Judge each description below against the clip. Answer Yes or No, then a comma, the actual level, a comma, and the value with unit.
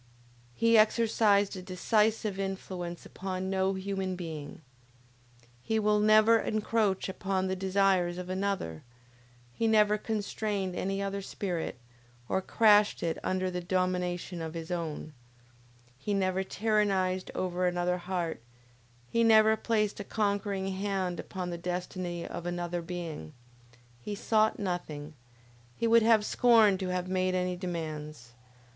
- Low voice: No, high, 190 Hz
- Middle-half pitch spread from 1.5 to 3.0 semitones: Yes, average, 2.7 semitones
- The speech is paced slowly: Yes, slow, 130 wpm